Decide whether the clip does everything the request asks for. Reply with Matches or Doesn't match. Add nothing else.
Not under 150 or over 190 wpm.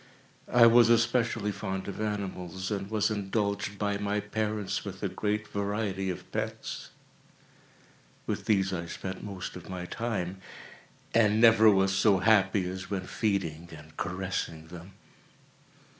Doesn't match